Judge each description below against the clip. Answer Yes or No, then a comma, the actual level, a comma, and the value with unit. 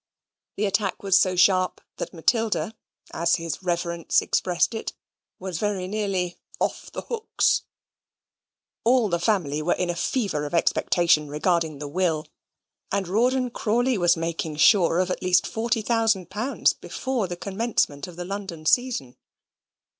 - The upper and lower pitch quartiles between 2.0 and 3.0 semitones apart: No, average, 4.0 semitones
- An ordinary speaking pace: Yes, average, 145 wpm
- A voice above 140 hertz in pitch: Yes, medium, 185 Hz